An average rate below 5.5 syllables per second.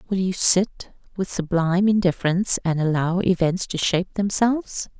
Yes: 5.2 syllables/s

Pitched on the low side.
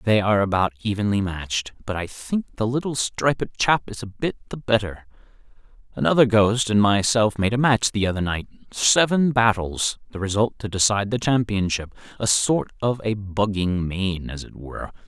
Yes: low, 105 Hz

